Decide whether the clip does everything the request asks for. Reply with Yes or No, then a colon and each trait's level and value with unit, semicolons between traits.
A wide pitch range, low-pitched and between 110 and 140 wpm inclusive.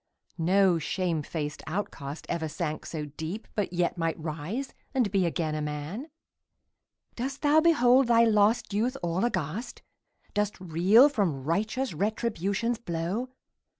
No: wide, 6.3 semitones; high, 195 Hz; slow, 135 wpm